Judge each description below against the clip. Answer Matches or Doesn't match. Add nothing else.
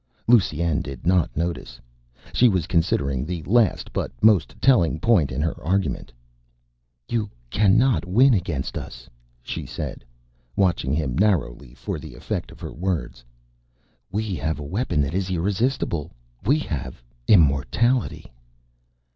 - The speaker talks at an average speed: Doesn't match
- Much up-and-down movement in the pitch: Matches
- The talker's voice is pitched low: Matches